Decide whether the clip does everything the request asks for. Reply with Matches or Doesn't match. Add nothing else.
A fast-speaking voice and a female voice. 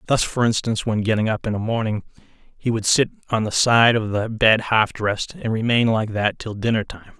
Doesn't match